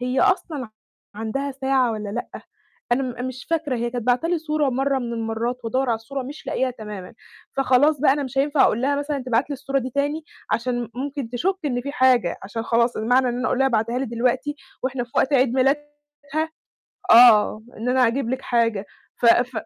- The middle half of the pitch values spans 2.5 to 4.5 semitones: Yes, average, 2.8 semitones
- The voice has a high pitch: Yes, very high, 255 Hz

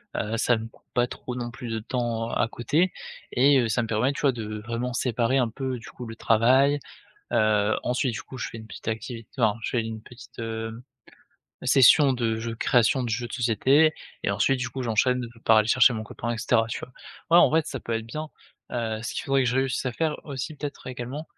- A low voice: Yes, low, 120 Hz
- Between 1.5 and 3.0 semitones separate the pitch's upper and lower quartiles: Yes, average, 2.7 semitones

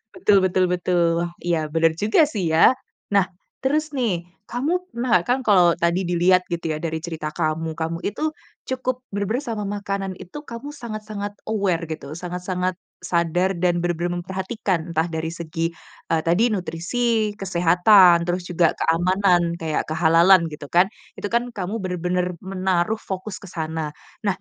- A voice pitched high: No, medium, 180 Hz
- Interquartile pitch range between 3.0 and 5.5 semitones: Yes, average, 3.4 semitones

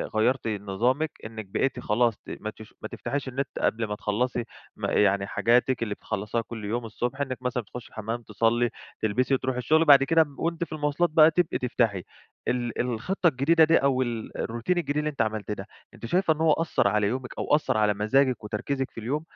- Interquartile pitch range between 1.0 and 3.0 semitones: No, average, 4.4 semitones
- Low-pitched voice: Yes, low, 125 Hz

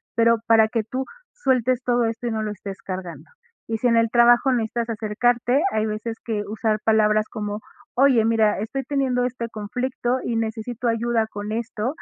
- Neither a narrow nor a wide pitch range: No, narrow, 2.0 semitones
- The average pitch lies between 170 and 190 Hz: No, high, 230 Hz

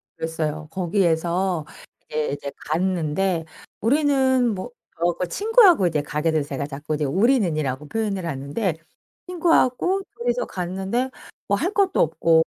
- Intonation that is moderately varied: No, wide, 7.8 semitones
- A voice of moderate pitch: Yes, medium, 180 Hz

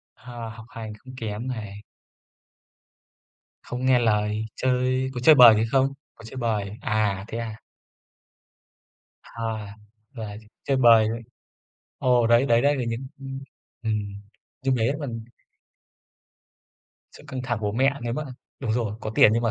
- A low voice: Yes, low, 115 Hz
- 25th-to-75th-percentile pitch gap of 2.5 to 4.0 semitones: Yes, average, 2.8 semitones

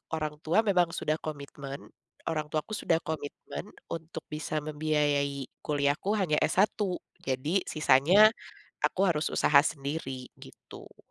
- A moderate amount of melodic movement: No, narrow, 2.3 semitones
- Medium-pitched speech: Yes, medium, 155 Hz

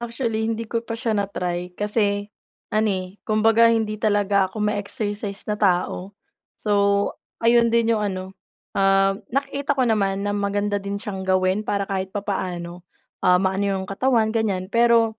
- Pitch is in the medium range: No, high, 205 Hz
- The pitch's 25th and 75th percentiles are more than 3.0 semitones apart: No, narrow, 2.5 semitones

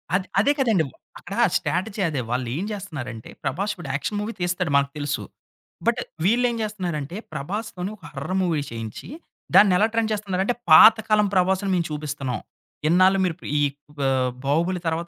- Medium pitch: Yes, medium, 180 Hz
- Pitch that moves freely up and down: Yes, wide, 5.7 semitones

